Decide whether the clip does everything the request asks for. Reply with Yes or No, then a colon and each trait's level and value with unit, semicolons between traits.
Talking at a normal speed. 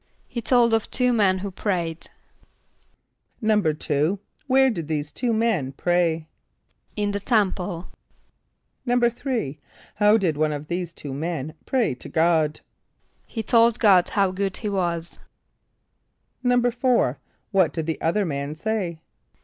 No: slow, 130 wpm